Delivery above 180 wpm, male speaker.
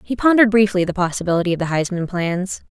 No: average, 200 wpm; female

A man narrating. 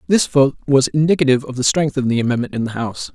Yes: male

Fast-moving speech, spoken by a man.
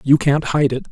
Yes: fast, 260 wpm; male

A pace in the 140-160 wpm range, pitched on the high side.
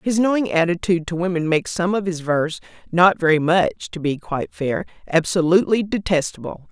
No: average, 150 wpm; medium, 175 Hz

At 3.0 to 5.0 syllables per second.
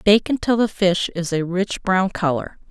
Yes: 4.5 syllables/s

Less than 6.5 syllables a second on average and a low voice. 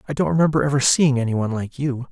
No: 6.8 syllables/s; low, 130 Hz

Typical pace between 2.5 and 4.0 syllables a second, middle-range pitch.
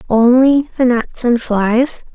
No: 3.3 syllables/s; high, 245 Hz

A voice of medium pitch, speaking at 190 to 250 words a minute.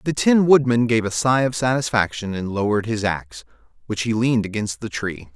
No: low, 115 Hz; average, 200 wpm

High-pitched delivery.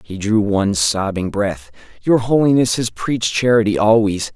No: low, 105 Hz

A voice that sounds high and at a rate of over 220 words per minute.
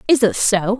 Yes: high, 220 Hz; fast, 230 wpm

